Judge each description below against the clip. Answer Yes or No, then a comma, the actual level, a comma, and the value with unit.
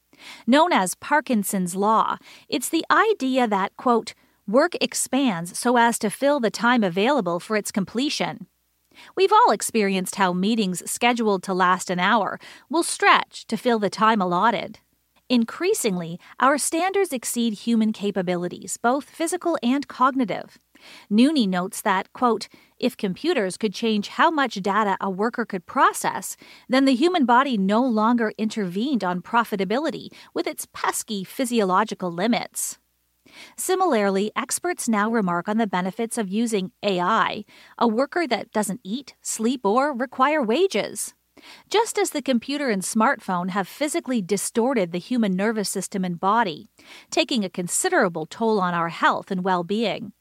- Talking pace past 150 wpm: No, average, 145 wpm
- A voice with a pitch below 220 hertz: No, high, 230 Hz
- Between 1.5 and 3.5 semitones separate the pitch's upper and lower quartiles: No, average, 5.3 semitones